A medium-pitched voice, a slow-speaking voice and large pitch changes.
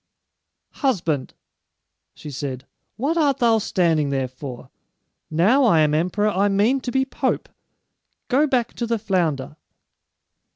No: high, 195 Hz; slow, 130 wpm; wide, 8.4 semitones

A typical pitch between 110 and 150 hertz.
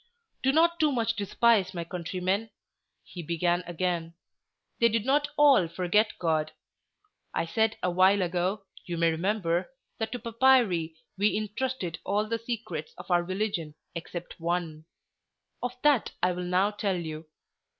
No: medium, 185 Hz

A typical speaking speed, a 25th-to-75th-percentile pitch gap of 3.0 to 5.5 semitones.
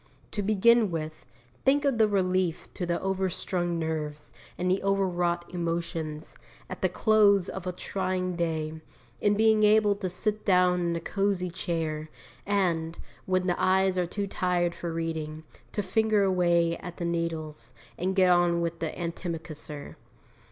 No: average, 160 wpm; narrow, 2.6 semitones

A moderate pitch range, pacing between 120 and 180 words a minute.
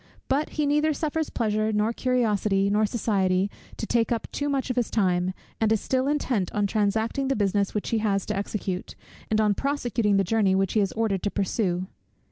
No: average, 3.6 semitones; average, 200 wpm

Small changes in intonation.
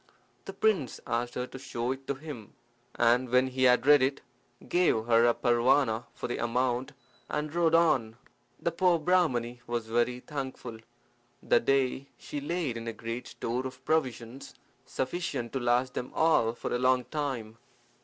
No: average, 3.4 semitones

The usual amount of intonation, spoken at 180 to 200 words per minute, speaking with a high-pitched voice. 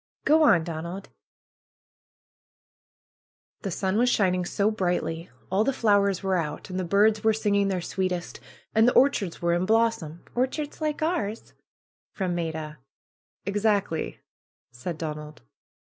No: average, 4.2 semitones; slow, 135 wpm; high, 195 Hz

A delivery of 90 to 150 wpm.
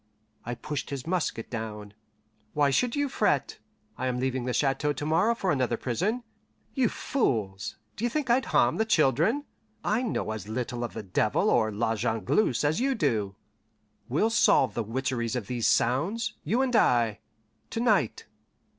No: average, 165 wpm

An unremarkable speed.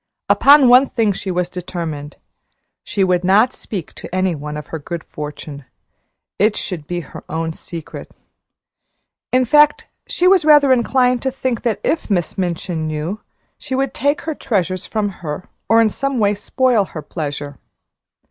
Yes: average, 165 wpm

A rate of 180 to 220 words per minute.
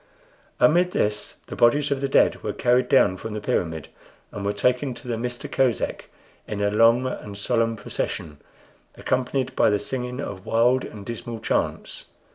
No: average, 170 wpm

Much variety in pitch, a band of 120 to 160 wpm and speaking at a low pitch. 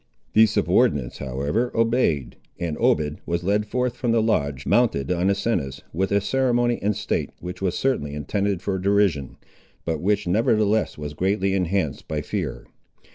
Yes: wide, 6.2 semitones; average, 155 wpm; very low, 95 Hz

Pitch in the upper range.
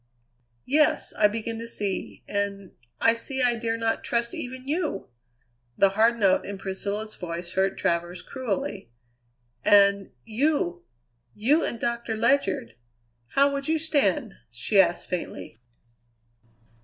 Yes: high, 220 Hz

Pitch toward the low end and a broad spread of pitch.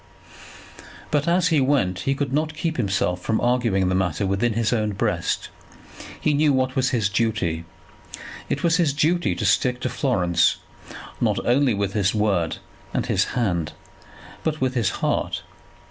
Yes: low, 120 Hz; wide, 6.7 semitones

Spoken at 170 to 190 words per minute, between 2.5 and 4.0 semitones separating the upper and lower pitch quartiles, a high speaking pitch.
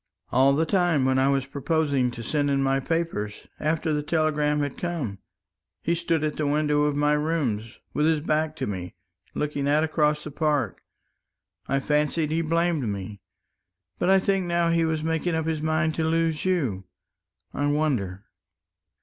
No: average, 175 wpm; average, 2.8 semitones; medium, 150 Hz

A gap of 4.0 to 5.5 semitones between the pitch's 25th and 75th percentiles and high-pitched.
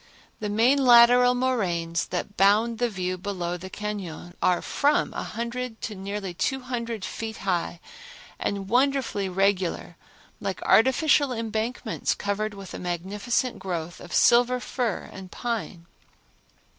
Yes: average, 4.5 semitones; high, 210 Hz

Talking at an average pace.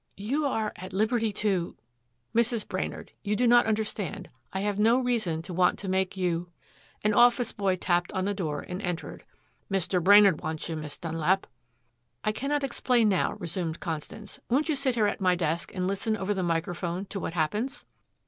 Yes: average, 190 wpm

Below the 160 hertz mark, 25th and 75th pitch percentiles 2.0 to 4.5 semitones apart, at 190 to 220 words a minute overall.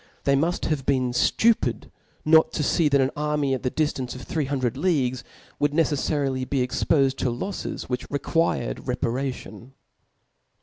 No: medium, 140 Hz; average, 2.8 semitones; average, 150 wpm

